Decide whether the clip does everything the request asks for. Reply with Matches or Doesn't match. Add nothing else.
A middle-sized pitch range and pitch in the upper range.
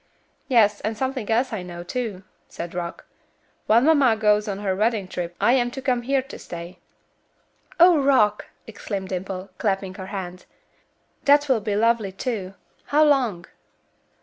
Matches